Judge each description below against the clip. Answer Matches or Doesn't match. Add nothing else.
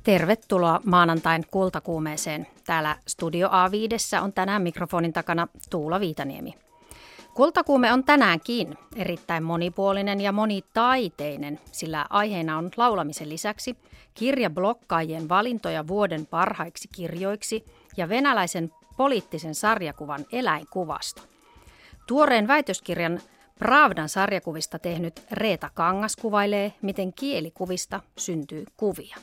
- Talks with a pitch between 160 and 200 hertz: Matches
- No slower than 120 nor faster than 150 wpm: Doesn't match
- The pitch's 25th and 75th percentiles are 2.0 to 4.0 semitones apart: Doesn't match